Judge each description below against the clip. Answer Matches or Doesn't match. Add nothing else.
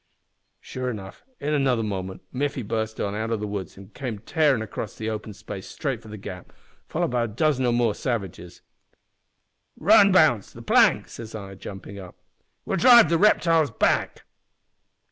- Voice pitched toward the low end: Matches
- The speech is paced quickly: Doesn't match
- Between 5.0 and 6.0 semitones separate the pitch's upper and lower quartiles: Matches